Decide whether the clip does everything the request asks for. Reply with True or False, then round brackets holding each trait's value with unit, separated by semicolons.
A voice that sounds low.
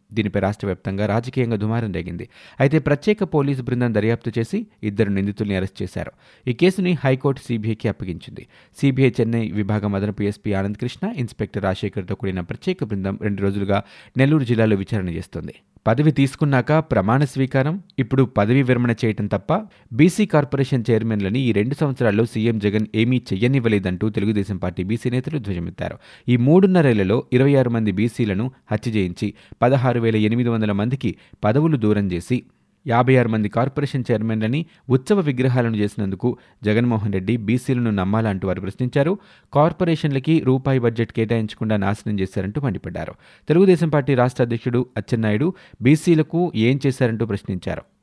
True (115 Hz)